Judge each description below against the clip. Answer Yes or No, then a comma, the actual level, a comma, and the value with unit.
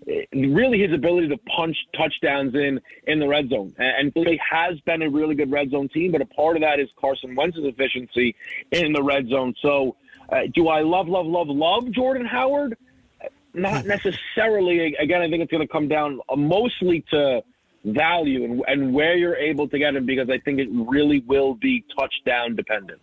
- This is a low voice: No, medium, 155 Hz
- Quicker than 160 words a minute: Yes, average, 195 wpm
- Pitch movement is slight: No, average, 4.1 semitones